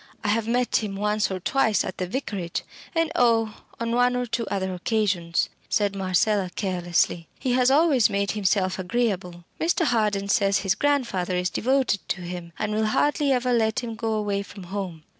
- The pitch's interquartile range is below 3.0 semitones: No, average, 4.3 semitones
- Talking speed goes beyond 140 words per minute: Yes, average, 180 wpm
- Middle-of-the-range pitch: No, high, 210 Hz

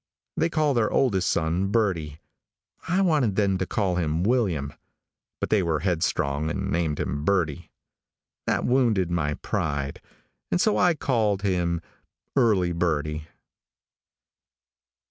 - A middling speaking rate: No, slow, 125 wpm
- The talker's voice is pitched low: Yes, very low, 90 Hz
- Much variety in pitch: Yes, wide, 6.1 semitones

